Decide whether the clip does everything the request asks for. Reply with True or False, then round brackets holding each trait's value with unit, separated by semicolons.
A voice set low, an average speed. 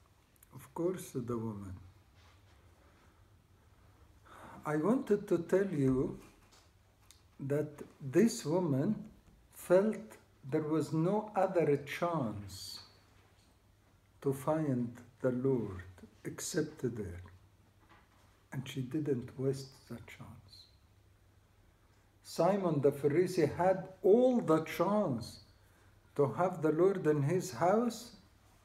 False (120 Hz; 90 wpm)